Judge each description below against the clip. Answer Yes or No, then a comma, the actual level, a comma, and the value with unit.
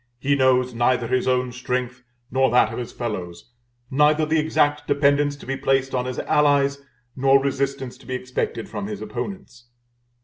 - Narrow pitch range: Yes, narrow, 2.2 semitones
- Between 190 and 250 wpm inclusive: No, average, 170 wpm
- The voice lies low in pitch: Yes, low, 130 Hz